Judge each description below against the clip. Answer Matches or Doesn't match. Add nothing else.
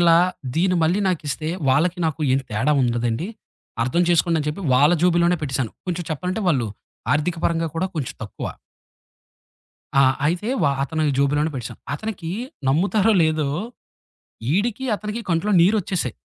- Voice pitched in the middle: Matches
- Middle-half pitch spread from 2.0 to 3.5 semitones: Doesn't match